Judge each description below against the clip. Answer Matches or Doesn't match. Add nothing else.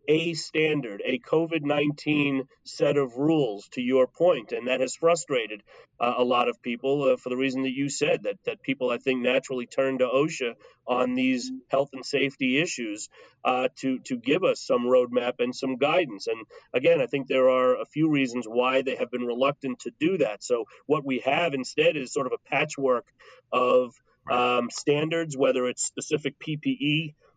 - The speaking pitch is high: Doesn't match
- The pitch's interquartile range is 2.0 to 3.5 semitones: Doesn't match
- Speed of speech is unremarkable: Matches